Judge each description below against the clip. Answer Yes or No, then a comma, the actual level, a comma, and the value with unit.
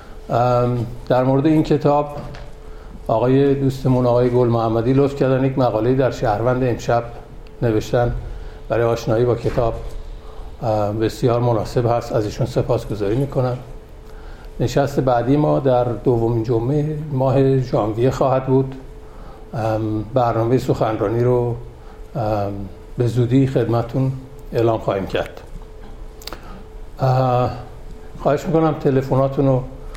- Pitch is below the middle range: Yes, low, 125 Hz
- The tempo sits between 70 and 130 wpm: Yes, slow, 105 wpm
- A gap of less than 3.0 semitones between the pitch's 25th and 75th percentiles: Yes, narrow, 2.6 semitones